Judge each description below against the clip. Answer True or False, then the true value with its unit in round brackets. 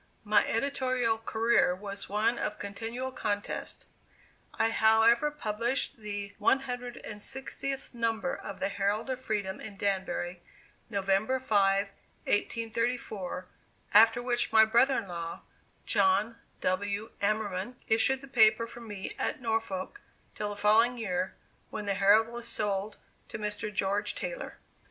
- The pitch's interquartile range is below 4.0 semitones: True (2.8 semitones)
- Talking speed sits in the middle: False (130 wpm)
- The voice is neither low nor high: False (220 Hz)